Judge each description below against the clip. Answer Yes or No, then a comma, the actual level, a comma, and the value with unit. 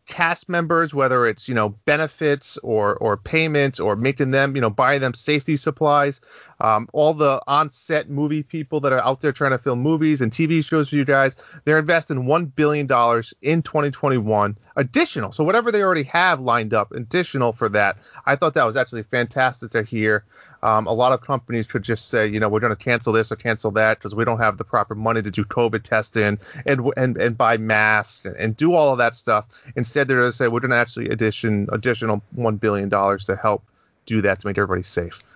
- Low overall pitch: Yes, low, 125 Hz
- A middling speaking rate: No, fast, 215 wpm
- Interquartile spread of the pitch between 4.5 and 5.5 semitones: Yes, average, 5.0 semitones